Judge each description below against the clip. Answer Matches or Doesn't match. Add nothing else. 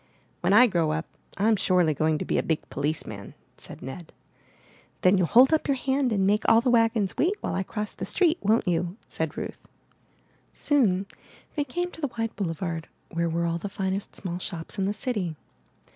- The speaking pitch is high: Matches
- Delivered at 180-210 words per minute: Matches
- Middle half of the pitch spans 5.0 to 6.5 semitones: Matches